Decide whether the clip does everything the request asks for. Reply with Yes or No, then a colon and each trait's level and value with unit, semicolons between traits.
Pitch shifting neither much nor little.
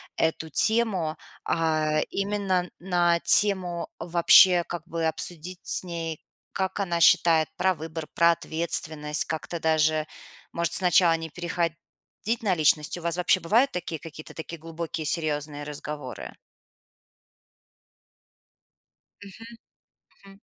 No: narrow, 2.2 semitones